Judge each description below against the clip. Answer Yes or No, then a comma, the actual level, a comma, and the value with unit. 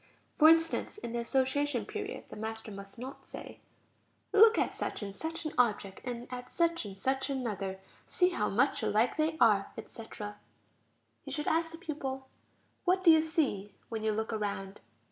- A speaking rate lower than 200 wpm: Yes, average, 175 wpm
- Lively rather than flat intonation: Yes, wide, 7.0 semitones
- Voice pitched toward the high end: Yes, very high, 250 Hz